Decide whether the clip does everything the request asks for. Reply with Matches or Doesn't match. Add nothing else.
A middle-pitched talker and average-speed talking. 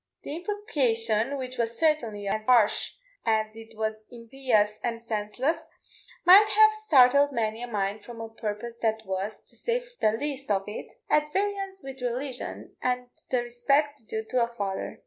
Doesn't match